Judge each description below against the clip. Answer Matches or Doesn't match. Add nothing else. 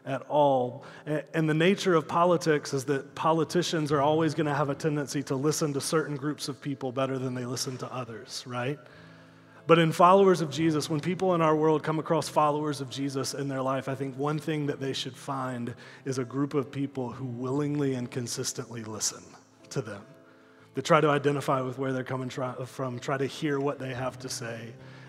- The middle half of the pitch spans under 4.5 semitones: Matches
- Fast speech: Matches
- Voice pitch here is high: Doesn't match